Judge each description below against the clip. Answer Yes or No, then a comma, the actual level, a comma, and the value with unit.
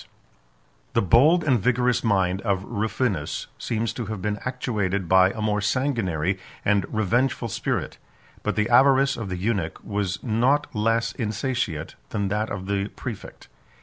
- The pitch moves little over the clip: No, average, 3.9 semitones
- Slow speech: No, average, 150 wpm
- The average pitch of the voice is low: Yes, low, 105 Hz